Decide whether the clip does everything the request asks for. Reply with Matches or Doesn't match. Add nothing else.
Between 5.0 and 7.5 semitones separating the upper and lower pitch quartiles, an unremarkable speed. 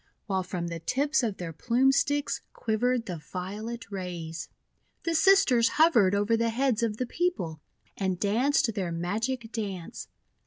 Matches